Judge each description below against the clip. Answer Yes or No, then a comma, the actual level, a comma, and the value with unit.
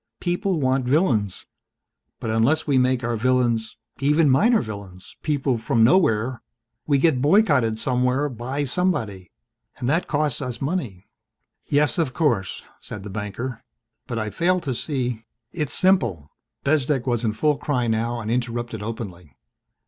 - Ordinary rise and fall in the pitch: Yes, average, 4.7 semitones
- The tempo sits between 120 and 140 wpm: No, average, 150 wpm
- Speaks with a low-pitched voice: Yes, low, 125 Hz